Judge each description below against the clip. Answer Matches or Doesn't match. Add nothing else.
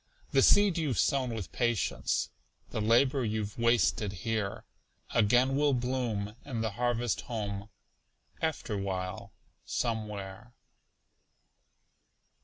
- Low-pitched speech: Matches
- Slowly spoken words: Matches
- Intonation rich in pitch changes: Doesn't match